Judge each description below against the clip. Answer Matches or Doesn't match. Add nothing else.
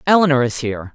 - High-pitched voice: Doesn't match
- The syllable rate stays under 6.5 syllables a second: Doesn't match